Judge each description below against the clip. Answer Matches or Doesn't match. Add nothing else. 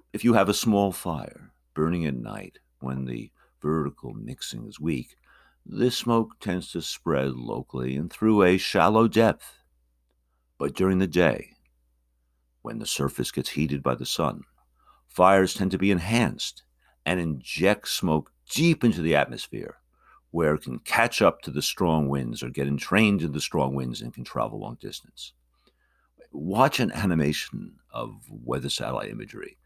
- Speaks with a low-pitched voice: Matches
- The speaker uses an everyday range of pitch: Doesn't match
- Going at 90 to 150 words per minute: Doesn't match